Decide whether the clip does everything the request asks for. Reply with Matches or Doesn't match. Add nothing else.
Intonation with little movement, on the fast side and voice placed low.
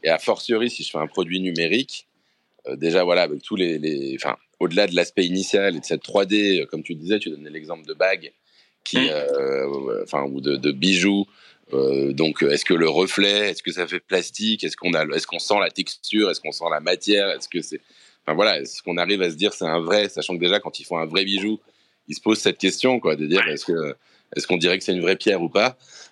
Doesn't match